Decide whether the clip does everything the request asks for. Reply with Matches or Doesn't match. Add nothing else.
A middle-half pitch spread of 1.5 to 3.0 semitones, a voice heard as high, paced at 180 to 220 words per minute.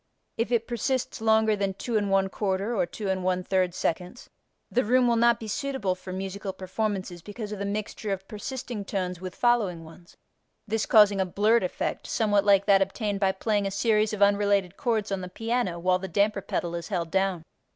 Matches